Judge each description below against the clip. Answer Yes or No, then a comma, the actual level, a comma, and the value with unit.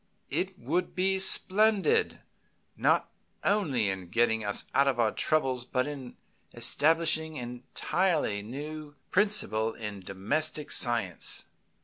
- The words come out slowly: Yes, slow, 115 wpm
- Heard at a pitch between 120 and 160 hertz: Yes, medium, 140 Hz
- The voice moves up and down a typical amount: No, wide, 7.8 semitones